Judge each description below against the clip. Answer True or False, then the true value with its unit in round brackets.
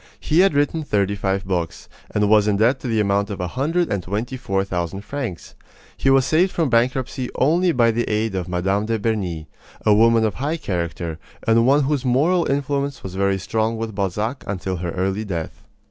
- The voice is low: True (110 Hz)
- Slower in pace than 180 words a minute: False (200 wpm)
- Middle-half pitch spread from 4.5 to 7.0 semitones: True (5.6 semitones)